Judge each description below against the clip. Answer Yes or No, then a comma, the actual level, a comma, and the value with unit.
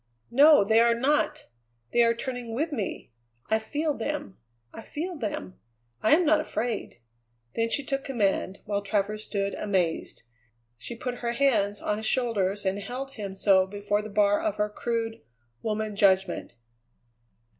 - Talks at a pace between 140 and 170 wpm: Yes, average, 155 wpm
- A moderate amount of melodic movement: Yes, average, 4.3 semitones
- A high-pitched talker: Yes, high, 220 Hz